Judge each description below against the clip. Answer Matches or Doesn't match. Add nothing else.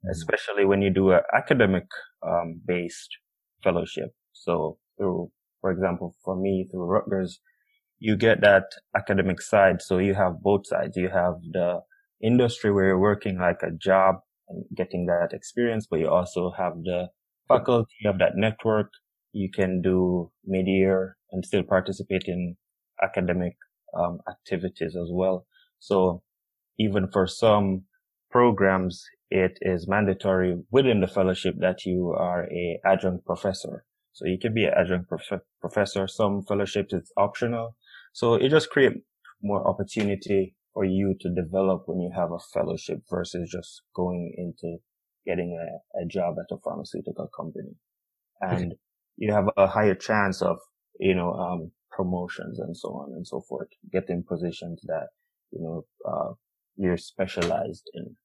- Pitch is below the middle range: Matches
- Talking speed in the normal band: Matches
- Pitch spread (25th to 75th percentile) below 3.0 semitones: Matches